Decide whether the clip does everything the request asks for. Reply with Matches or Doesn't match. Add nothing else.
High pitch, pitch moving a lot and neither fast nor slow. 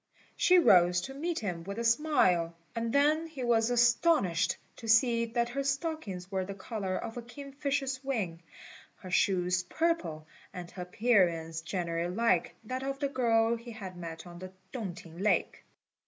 Matches